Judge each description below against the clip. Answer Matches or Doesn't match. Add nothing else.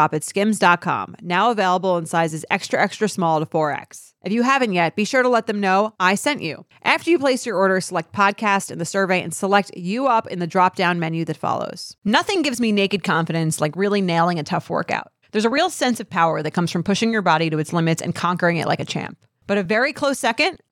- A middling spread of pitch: Matches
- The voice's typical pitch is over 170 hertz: Matches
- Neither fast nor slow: Doesn't match